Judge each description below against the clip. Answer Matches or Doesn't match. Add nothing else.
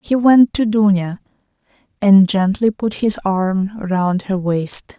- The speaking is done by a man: Doesn't match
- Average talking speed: Matches